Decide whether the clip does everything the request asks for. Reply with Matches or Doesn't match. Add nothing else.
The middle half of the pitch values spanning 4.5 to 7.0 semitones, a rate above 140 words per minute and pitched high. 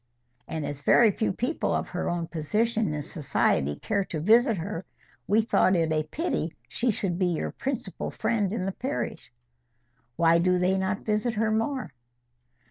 Matches